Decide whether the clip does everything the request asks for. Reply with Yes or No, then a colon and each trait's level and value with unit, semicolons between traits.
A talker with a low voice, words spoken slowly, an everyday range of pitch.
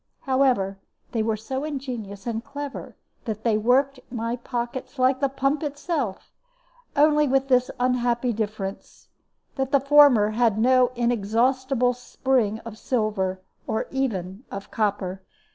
No: high, 245 Hz; slow, 130 wpm; average, 3.7 semitones